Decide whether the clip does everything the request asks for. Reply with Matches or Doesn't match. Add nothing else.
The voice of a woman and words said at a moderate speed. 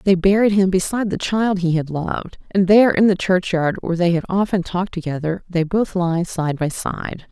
Doesn't match